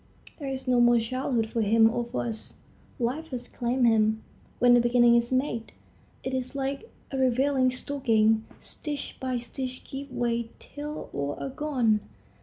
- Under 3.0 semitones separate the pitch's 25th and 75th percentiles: Yes, narrow, 2.4 semitones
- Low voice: No, high, 245 Hz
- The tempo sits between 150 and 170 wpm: Yes, average, 165 wpm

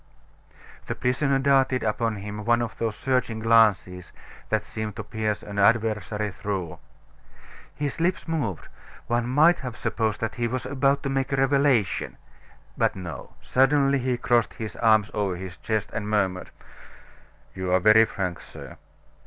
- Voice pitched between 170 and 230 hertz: No, low, 115 Hz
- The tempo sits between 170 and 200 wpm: No, average, 155 wpm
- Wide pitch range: No, average, 4.1 semitones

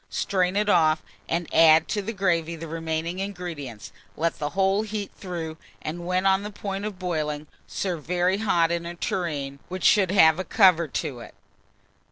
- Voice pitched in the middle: Yes, medium, 175 Hz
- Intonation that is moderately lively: Yes, average, 3.2 semitones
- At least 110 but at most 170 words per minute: No, average, 180 wpm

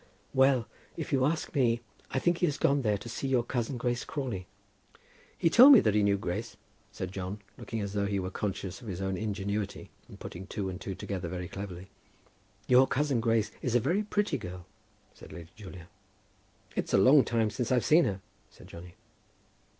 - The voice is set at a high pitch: No, low, 110 Hz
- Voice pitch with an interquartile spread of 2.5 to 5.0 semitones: No, wide, 5.5 semitones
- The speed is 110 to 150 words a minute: No, average, 195 wpm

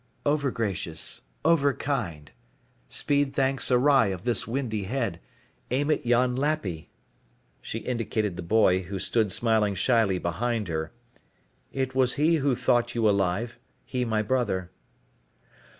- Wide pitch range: No, average, 5.0 semitones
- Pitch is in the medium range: No, low, 120 Hz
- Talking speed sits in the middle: No, slow, 125 wpm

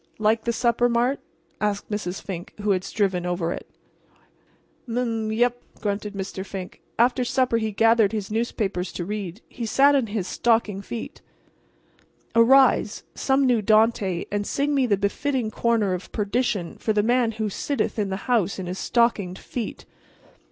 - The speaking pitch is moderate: No, high, 220 Hz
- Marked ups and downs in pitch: No, average, 3.2 semitones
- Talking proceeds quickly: No, average, 165 wpm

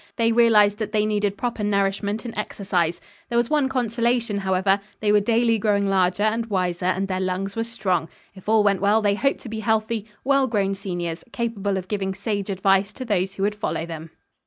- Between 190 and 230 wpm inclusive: Yes, fast, 205 wpm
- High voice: Yes, high, 205 Hz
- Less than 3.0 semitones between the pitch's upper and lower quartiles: Yes, narrow, 2.6 semitones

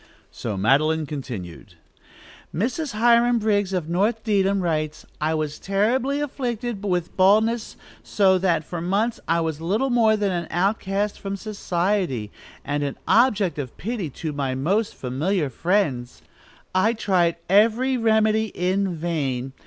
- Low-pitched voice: No, high, 190 Hz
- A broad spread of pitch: Yes, wide, 5.7 semitones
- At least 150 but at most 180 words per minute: No, slow, 135 wpm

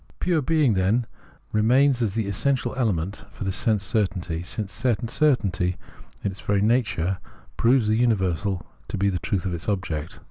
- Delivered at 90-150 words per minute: No, average, 170 wpm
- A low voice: Yes, low, 105 Hz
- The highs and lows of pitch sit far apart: No, average, 4.3 semitones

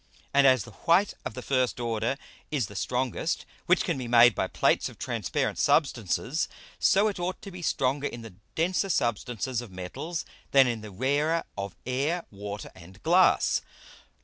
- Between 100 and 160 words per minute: No, average, 175 wpm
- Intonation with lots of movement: Yes, wide, 6.0 semitones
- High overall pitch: No, low, 130 Hz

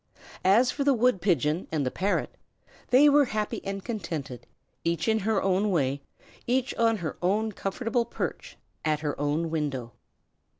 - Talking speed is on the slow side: No, average, 160 wpm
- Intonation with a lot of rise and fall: Yes, wide, 6.7 semitones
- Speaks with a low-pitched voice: No, high, 195 Hz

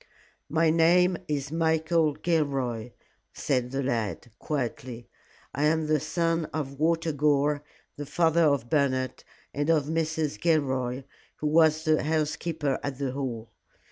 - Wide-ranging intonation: No, average, 2.9 semitones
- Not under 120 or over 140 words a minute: Yes, slow, 135 wpm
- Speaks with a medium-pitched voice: Yes, medium, 150 Hz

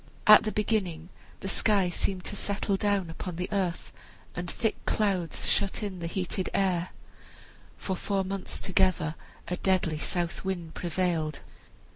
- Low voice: No, medium, 185 Hz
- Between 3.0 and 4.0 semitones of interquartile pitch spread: No, narrow, 2.4 semitones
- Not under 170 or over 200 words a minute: No, average, 145 wpm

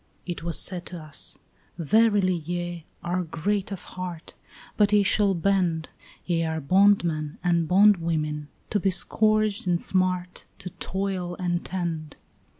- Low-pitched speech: No, medium, 180 Hz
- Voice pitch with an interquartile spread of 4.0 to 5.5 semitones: No, average, 2.9 semitones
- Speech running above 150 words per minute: No, average, 140 wpm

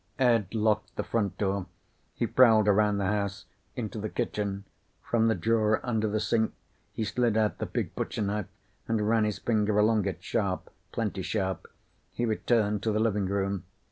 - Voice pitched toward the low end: Yes, low, 105 Hz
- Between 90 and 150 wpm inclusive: No, average, 175 wpm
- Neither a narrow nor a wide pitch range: No, narrow, 1.8 semitones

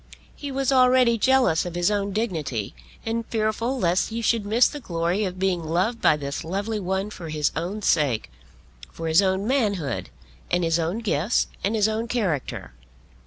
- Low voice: No, high, 200 Hz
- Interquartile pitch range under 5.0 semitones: No, average, 5.3 semitones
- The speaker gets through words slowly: No, average, 175 wpm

